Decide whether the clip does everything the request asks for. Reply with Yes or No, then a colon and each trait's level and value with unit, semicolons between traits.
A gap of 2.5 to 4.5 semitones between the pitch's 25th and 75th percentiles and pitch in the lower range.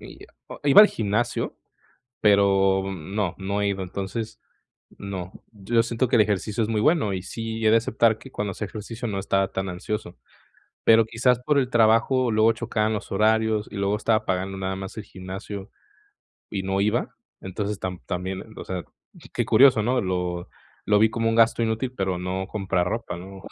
Yes: average, 2.9 semitones; low, 105 Hz